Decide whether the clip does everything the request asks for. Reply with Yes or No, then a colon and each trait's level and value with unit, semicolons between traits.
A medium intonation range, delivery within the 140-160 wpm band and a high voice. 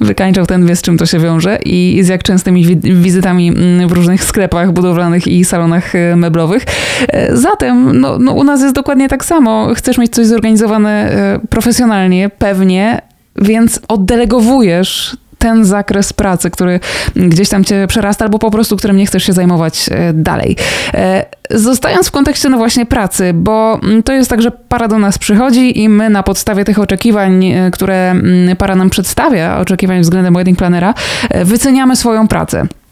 Yes: average, 4.0 semitones; average, 155 wpm; high, 195 Hz